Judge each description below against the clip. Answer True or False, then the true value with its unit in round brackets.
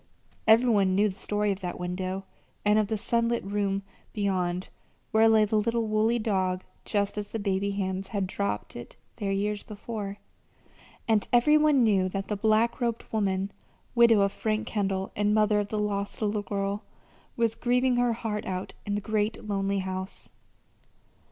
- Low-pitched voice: False (205 Hz)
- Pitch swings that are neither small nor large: False (2.0 semitones)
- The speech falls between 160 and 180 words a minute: True (170 wpm)